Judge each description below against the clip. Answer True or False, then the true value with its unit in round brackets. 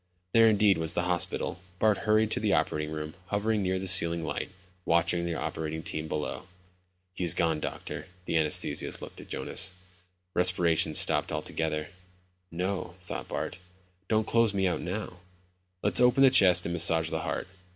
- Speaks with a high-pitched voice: False (90 Hz)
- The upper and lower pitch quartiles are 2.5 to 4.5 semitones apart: True (3.6 semitones)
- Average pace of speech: True (160 wpm)